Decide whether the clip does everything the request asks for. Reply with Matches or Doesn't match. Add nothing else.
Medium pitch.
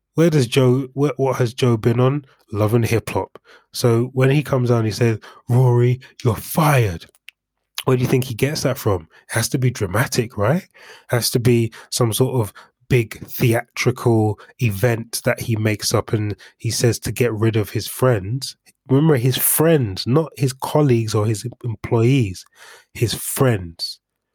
Doesn't match